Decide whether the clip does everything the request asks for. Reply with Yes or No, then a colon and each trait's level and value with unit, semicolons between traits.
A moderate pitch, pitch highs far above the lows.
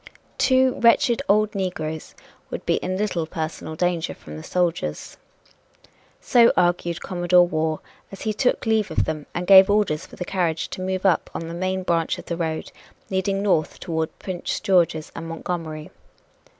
No: medium, 175 Hz; average, 3.2 semitones